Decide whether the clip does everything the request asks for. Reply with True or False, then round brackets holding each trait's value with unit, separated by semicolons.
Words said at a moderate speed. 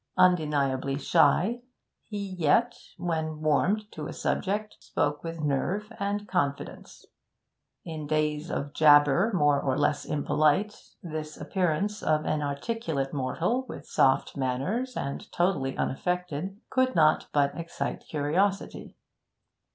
False (120 wpm)